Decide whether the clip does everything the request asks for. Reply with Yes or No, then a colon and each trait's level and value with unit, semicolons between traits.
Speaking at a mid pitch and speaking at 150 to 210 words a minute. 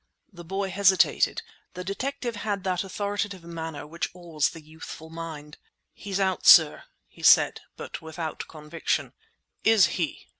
No: medium, 175 Hz; average, 140 wpm